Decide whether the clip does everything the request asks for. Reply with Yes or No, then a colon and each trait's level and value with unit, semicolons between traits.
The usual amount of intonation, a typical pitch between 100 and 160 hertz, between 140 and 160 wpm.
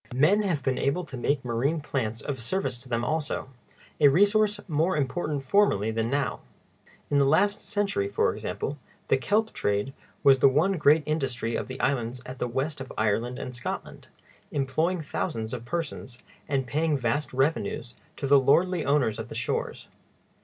No: average, 4.3 semitones; medium, 140 Hz; average, 170 wpm